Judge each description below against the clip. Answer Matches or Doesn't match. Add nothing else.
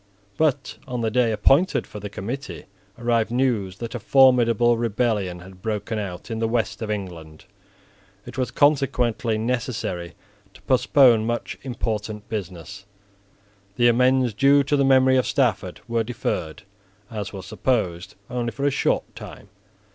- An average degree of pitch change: Matches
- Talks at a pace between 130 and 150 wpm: Matches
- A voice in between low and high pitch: Doesn't match